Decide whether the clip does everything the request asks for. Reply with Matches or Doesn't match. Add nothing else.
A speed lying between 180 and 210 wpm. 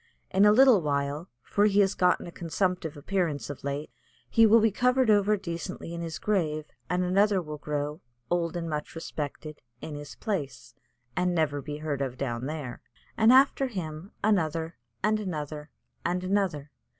Doesn't match